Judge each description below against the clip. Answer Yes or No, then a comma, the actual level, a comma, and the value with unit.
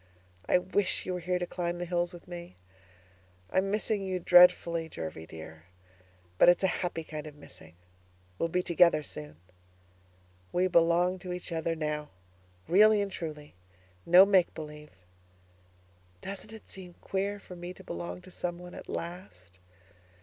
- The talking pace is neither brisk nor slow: Yes, average, 155 wpm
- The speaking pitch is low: No, medium, 175 Hz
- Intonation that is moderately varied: Yes, average, 3.0 semitones